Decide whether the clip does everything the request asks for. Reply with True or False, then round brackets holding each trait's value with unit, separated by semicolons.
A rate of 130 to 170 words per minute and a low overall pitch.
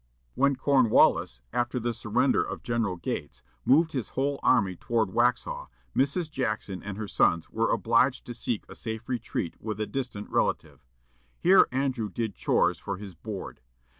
True (160 wpm; 120 Hz)